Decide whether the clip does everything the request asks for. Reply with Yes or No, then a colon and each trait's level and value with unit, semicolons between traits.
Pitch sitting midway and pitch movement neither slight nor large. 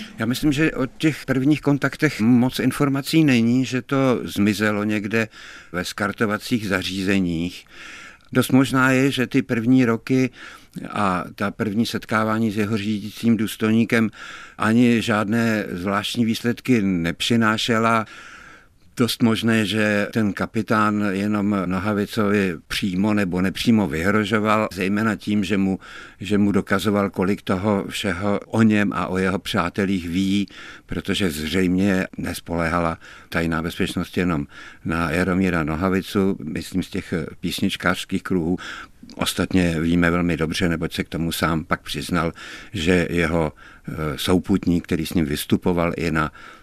No: low, 100 Hz; average, 3.9 semitones